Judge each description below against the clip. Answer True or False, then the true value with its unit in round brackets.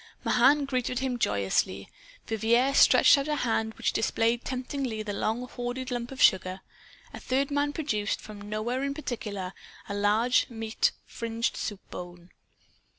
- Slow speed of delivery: False (150 wpm)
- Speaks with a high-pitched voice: True (230 Hz)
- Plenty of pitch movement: False (3.8 semitones)